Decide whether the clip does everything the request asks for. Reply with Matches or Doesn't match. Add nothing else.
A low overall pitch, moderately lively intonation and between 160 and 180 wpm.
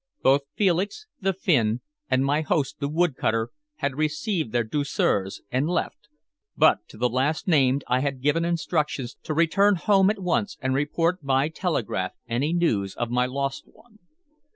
Doesn't match